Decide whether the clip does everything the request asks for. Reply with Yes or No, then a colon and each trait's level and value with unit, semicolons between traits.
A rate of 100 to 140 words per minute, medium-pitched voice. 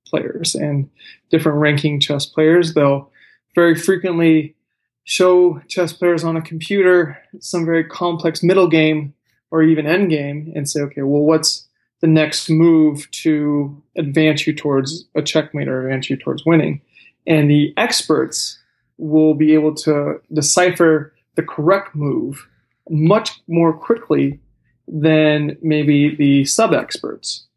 Yes: slow, 135 wpm; medium, 155 Hz